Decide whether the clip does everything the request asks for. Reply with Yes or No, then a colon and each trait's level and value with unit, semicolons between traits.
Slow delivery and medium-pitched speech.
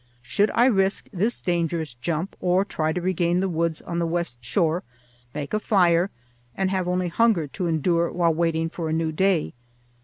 No: average, 185 wpm; medium, 170 Hz